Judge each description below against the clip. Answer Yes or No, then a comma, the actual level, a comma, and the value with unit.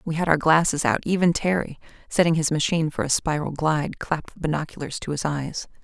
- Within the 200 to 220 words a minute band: Yes, fast, 205 wpm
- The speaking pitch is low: No, medium, 155 Hz